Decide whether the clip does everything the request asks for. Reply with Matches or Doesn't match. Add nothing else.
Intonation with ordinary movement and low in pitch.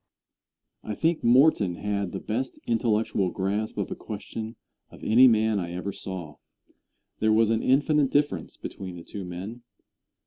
Matches